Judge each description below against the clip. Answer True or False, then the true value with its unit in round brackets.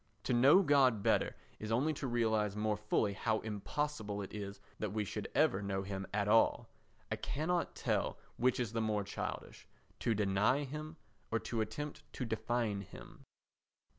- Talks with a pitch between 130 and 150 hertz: False (110 Hz)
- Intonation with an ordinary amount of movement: True (3.7 semitones)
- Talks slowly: False (165 wpm)